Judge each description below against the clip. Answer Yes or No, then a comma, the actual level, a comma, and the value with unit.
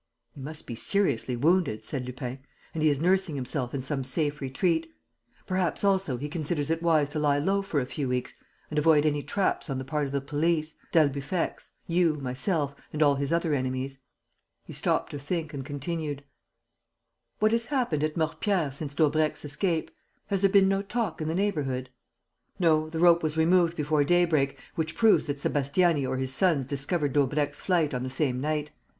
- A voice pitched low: No, medium, 150 Hz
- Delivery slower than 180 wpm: No, average, 185 wpm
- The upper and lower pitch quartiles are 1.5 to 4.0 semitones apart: Yes, average, 3.6 semitones